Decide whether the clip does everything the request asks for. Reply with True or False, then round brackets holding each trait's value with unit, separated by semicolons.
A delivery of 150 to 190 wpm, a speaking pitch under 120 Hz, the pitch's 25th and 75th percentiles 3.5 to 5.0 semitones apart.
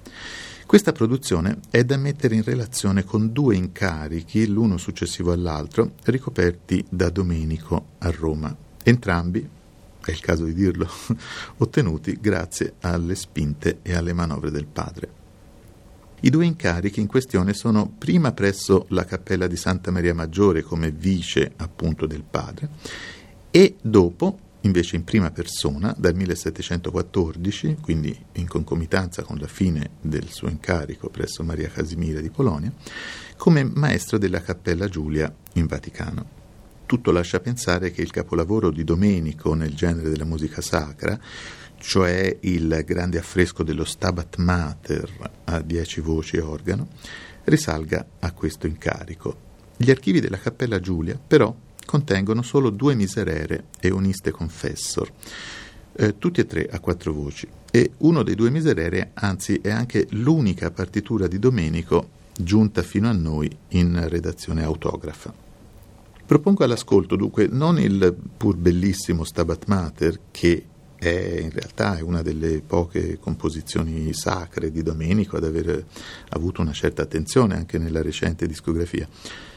False (135 wpm; 90 Hz; 4.2 semitones)